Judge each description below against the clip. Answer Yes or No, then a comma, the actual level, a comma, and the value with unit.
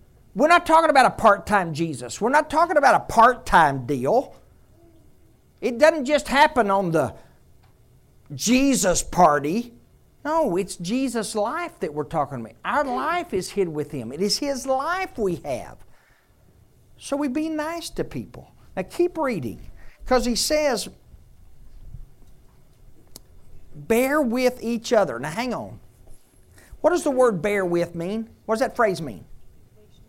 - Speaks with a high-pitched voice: Yes, high, 210 Hz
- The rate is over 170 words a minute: No, average, 150 wpm